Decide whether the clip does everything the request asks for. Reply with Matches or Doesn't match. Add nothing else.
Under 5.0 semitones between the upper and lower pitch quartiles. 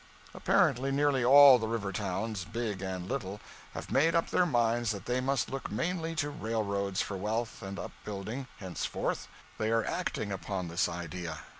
Doesn't match